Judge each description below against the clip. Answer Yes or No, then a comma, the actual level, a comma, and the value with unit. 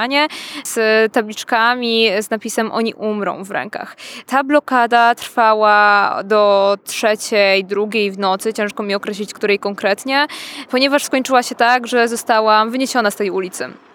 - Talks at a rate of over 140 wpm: No, average, 135 wpm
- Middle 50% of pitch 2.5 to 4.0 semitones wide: Yes, average, 3.1 semitones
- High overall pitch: Yes, high, 225 Hz